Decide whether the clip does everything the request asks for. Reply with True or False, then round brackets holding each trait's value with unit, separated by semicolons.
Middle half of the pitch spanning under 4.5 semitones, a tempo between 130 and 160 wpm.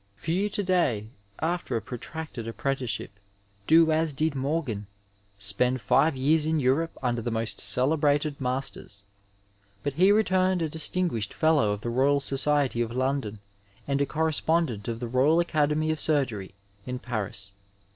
False (5.3 semitones; 145 wpm)